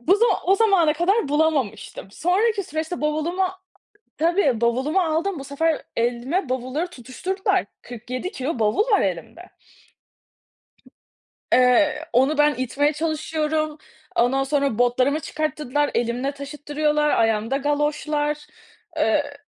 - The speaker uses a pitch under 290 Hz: No, very high, 295 Hz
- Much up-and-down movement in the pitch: No, average, 3.7 semitones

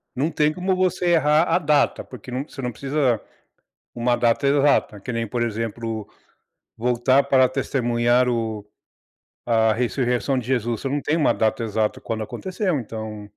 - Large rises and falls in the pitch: No, average, 3.9 semitones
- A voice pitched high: No, low, 125 Hz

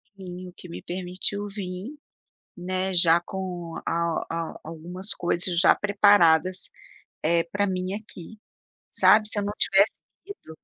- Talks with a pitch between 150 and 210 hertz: Yes, medium, 185 Hz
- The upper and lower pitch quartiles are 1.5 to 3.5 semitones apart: Yes, average, 2.7 semitones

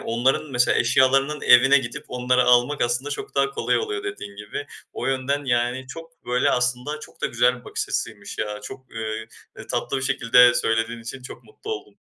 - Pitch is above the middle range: No, low, 125 Hz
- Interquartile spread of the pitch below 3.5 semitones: Yes, narrow, 2.5 semitones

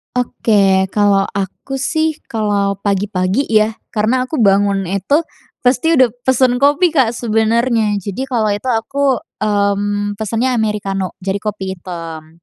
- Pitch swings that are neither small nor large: Yes, average, 3.9 semitones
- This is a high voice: Yes, high, 215 Hz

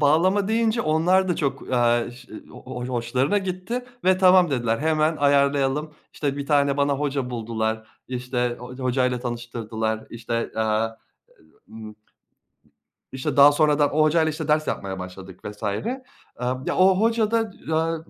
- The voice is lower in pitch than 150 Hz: Yes, medium, 140 Hz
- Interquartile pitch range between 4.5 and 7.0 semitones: Yes, average, 5.3 semitones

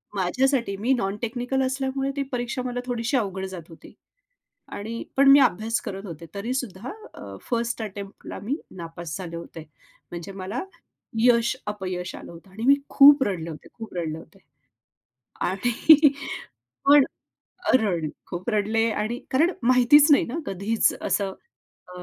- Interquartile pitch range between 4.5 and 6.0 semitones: Yes, average, 5.3 semitones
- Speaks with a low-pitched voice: No, high, 225 Hz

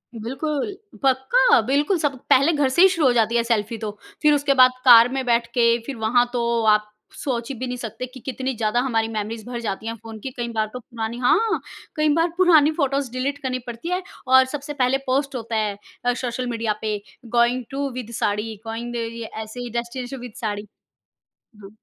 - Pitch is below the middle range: No, high, 245 Hz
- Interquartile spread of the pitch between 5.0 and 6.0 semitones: No, average, 3.1 semitones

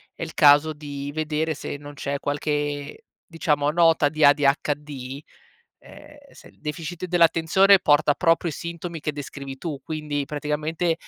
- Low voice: No, medium, 150 Hz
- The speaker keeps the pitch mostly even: Yes, narrow, 2.2 semitones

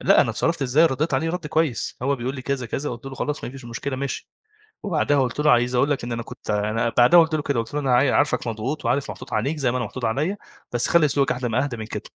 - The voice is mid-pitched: No, low, 130 Hz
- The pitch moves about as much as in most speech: Yes, average, 3.5 semitones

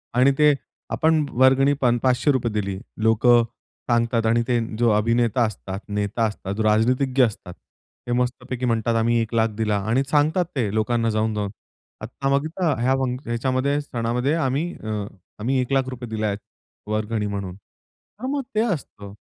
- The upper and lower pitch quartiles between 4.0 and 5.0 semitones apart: No, average, 3.5 semitones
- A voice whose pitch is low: Yes, low, 120 Hz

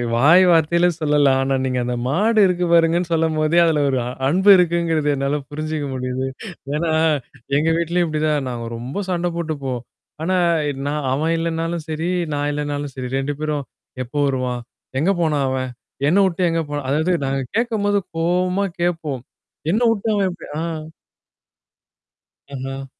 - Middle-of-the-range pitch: Yes, medium, 155 Hz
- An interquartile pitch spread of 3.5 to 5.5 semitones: Yes, average, 3.8 semitones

